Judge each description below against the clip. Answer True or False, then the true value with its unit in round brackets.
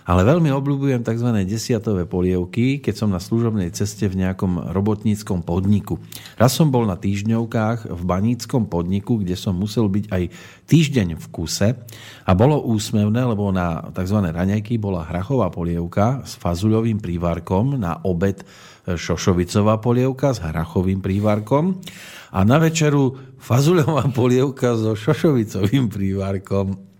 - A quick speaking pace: False (130 wpm)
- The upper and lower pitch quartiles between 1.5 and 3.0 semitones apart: False (4.6 semitones)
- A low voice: True (105 Hz)